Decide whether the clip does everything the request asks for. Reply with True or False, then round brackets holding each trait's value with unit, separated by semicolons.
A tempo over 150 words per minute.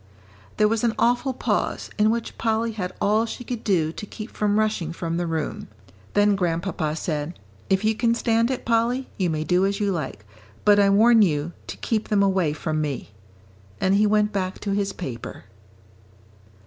True (185 wpm)